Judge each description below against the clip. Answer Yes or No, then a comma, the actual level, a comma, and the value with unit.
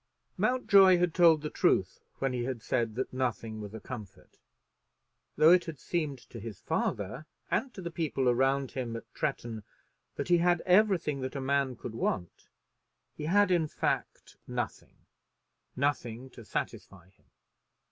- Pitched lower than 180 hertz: Yes, low, 135 Hz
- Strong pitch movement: Yes, wide, 6.2 semitones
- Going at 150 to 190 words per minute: Yes, average, 155 wpm